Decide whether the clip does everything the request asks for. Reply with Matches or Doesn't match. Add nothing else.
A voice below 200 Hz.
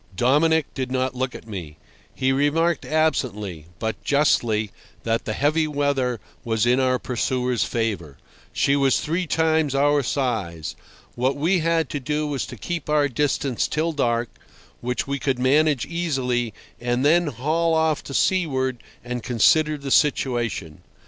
Matches